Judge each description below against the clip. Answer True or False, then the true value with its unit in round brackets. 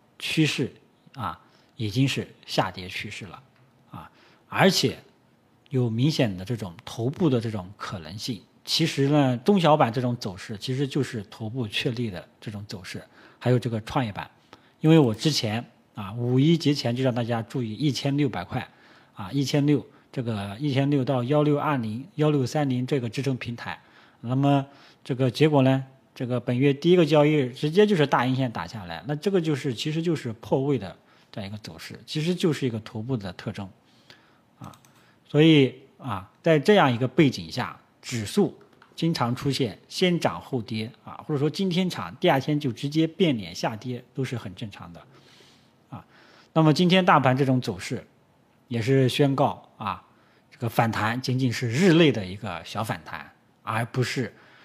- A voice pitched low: True (130 Hz)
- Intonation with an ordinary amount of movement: True (4.5 semitones)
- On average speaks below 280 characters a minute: True (260 characters per minute)